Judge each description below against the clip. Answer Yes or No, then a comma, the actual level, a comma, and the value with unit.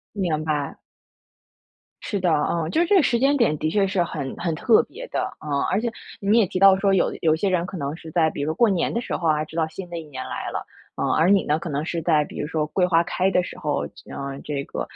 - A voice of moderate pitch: Yes, medium, 170 Hz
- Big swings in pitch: No, average, 4.2 semitones